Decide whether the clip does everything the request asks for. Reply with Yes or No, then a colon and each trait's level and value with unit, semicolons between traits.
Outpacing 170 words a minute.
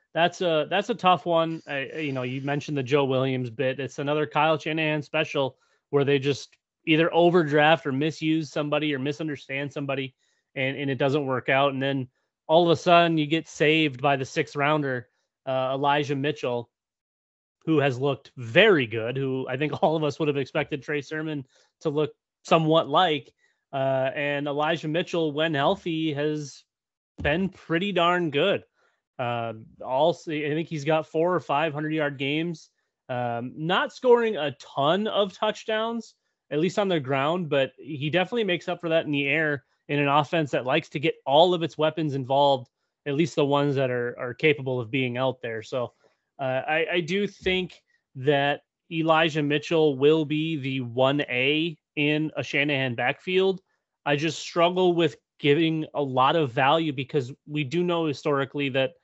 Yes: average, 180 wpm